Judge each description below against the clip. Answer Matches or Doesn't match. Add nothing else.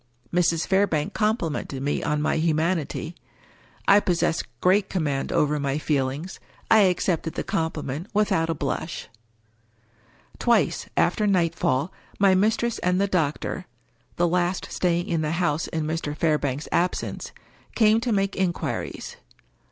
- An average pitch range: Matches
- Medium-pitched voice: Matches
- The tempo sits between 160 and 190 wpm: Doesn't match